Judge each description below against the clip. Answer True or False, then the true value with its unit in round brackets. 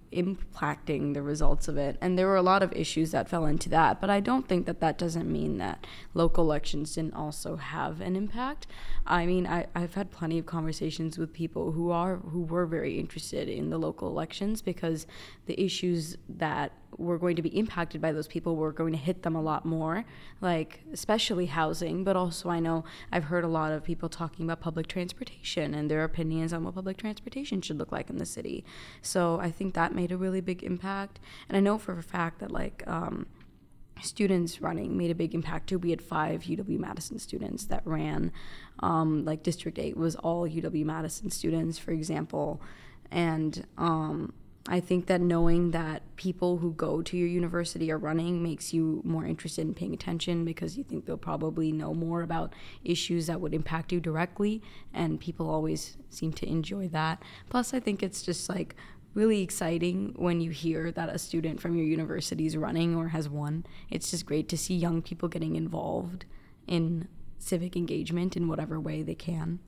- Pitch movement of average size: False (1.9 semitones)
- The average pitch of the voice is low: False (165 Hz)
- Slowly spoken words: False (195 wpm)